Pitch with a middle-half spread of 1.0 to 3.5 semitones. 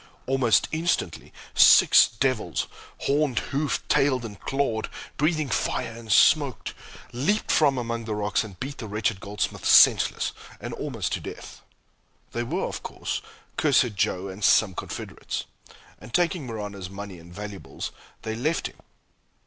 No: average, 5.3 semitones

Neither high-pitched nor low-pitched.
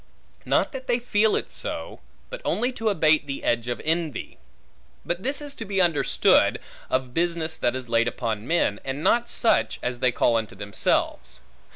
Yes: medium, 155 Hz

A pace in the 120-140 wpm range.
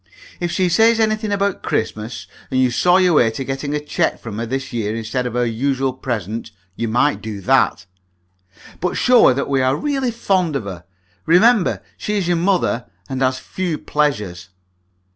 No: average, 185 wpm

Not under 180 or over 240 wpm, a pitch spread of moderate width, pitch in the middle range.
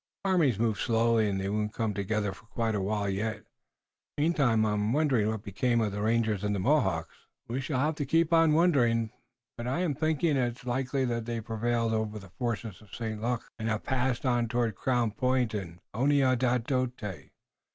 No: average, 185 wpm; average, 3.3 semitones; low, 115 Hz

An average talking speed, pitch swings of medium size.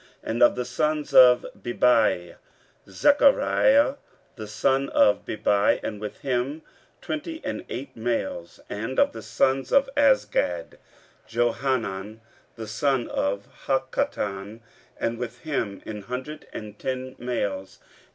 No: slow, 130 wpm; average, 4.3 semitones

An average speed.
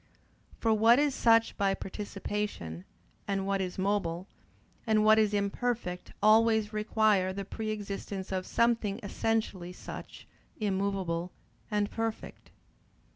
No: slow, 120 wpm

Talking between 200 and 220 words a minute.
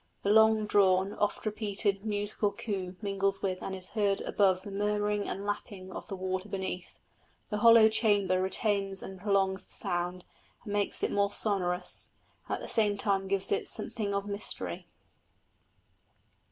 No: average, 160 wpm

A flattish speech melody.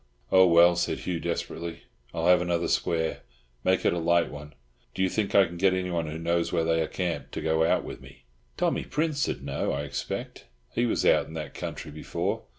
Yes: narrow, 2.1 semitones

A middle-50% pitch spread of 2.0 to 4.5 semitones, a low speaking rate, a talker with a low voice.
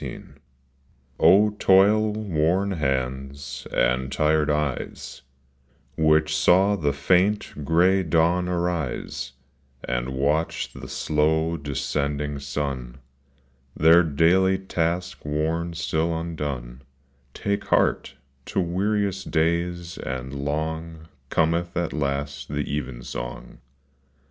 Yes: average, 3.7 semitones; slow, 100 wpm; very low, 80 Hz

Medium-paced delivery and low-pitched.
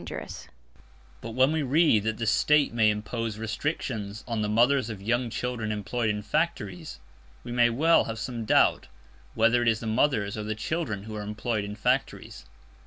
Yes: average, 175 wpm; low, 115 Hz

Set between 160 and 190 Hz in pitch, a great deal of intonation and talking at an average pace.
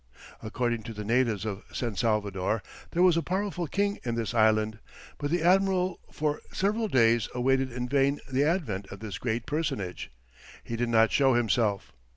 No: low, 120 Hz; wide, 6.2 semitones; average, 175 wpm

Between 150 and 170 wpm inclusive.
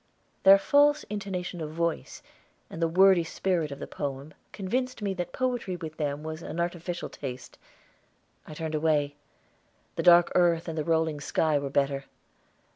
Yes: average, 160 wpm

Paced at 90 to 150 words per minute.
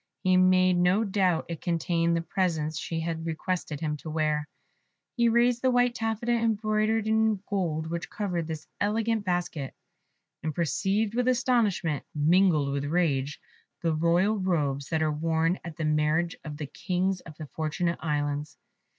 No: average, 160 wpm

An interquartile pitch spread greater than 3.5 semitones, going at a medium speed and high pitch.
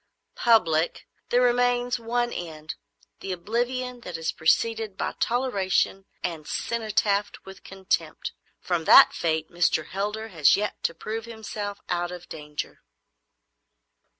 No: average, 5.3 semitones; slow, 125 wpm; high, 200 Hz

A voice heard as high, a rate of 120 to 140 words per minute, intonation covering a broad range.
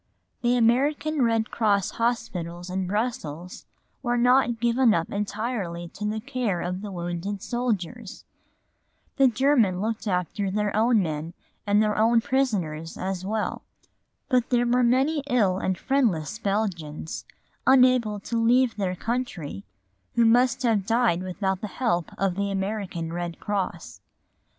No: high, 210 Hz; slow, 135 wpm; average, 4.8 semitones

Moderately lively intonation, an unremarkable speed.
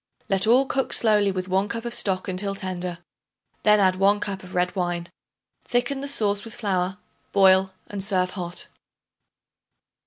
No: narrow, 2.2 semitones; average, 160 wpm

